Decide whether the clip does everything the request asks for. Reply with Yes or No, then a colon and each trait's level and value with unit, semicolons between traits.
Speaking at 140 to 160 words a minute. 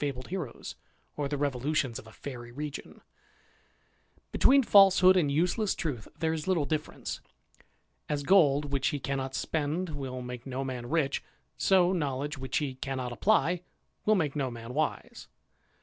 Yes: average, 150 wpm